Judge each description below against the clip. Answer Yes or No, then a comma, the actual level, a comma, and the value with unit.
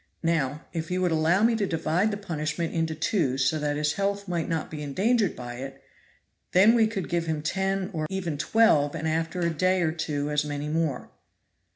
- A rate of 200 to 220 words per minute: Yes, fast, 205 wpm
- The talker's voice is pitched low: No, medium, 165 Hz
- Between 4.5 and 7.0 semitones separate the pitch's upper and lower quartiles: No, average, 4.1 semitones